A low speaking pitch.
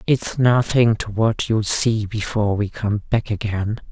Yes: low, 110 Hz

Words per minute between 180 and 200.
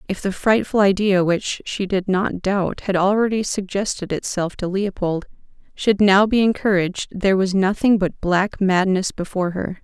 No: average, 165 wpm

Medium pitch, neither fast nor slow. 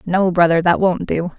No: medium, 175 Hz; fast, 215 wpm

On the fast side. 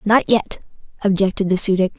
No: average, 180 wpm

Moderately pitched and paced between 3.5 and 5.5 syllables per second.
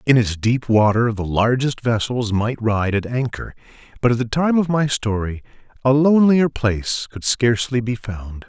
No: low, 120 Hz; 4.7 syllables/s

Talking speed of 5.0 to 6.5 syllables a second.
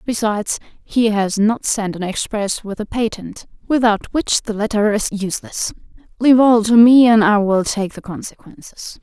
No: 4.8 syllables/s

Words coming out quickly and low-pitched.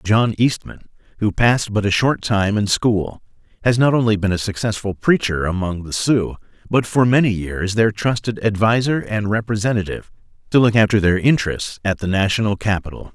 No: average, 175 wpm; low, 105 Hz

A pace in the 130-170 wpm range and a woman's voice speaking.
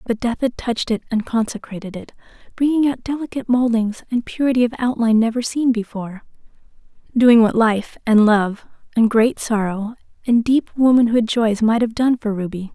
Yes: average, 165 wpm; female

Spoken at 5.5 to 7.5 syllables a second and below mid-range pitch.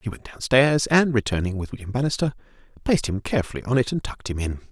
Yes: 6.8 syllables/s; low, 120 Hz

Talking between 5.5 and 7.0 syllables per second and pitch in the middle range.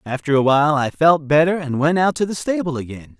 Yes: 5.9 syllables/s; medium, 150 Hz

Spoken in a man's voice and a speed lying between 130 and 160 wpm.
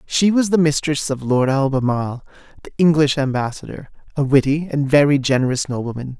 Yes: male; average, 155 wpm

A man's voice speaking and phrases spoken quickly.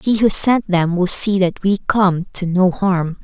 No: female; fast, 220 wpm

